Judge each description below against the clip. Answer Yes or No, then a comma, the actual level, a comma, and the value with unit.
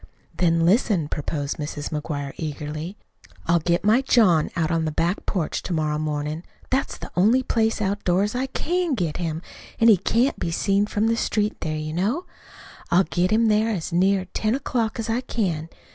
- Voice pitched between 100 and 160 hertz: No, medium, 185 Hz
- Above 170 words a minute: Yes, average, 185 wpm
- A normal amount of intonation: No, wide, 5.7 semitones